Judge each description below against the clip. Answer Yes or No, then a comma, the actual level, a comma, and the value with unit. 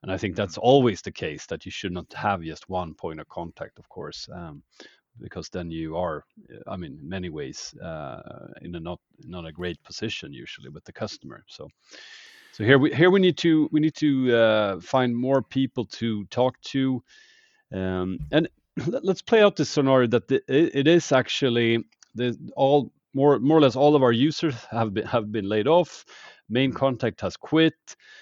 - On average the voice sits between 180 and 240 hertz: No, low, 130 Hz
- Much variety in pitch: Yes, wide, 6.6 semitones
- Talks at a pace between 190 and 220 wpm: Yes, average, 200 wpm